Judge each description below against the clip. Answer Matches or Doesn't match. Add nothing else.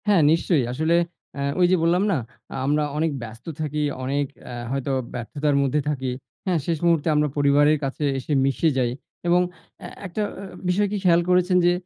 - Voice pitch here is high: Doesn't match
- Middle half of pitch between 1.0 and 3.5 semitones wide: Doesn't match